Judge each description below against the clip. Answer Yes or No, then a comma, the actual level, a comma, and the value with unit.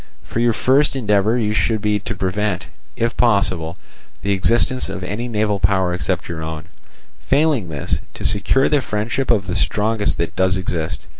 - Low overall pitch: Yes, low, 105 Hz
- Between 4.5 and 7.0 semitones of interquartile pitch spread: No, average, 4.1 semitones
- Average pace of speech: Yes, average, 165 wpm